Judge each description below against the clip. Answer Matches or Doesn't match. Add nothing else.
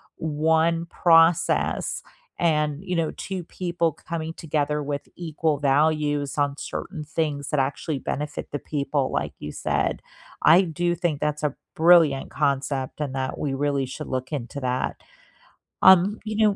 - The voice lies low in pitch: Doesn't match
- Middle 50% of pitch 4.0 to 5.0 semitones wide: Doesn't match